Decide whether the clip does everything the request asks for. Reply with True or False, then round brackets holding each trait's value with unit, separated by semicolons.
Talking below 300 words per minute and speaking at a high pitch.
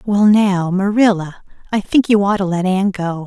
True (200 wpm; 195 Hz)